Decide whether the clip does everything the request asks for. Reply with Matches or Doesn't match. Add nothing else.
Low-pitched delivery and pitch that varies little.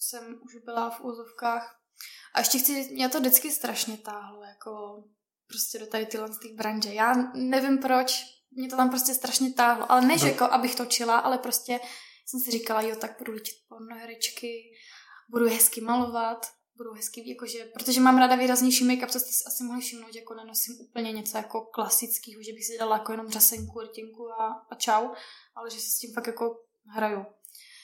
Doesn't match